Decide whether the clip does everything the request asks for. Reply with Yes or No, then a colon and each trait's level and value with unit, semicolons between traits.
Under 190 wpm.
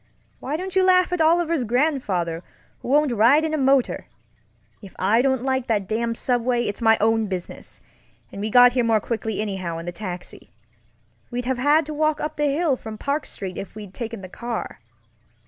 No: average, 195 wpm